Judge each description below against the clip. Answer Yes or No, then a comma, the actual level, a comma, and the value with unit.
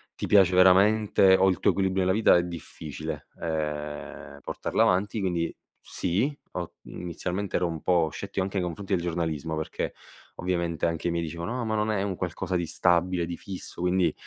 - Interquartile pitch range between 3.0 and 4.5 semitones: No, narrow, 2.4 semitones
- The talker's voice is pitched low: Yes, very low, 90 Hz